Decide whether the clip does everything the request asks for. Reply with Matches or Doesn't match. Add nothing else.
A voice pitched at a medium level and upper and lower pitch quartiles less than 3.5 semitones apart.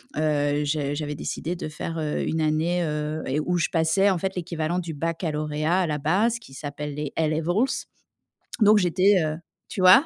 Matches